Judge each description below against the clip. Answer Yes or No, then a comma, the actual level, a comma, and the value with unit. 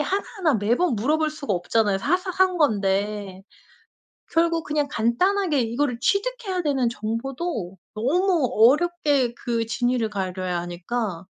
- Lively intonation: Yes, wide, 7.8 semitones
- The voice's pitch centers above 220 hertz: Yes, very high, 250 Hz